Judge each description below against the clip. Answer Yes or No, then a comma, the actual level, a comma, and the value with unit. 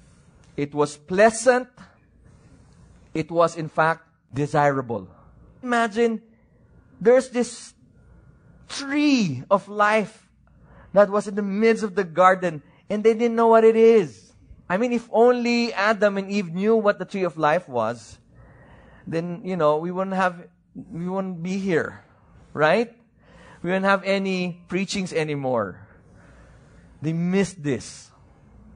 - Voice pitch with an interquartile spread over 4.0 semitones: Yes, wide, 5.4 semitones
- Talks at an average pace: No, slow, 130 wpm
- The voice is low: No, high, 190 Hz